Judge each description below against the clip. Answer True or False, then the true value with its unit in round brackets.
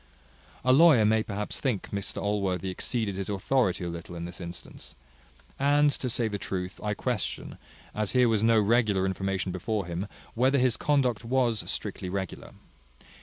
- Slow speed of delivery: False (165 wpm)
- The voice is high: False (105 Hz)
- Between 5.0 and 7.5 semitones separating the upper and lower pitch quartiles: False (4.5 semitones)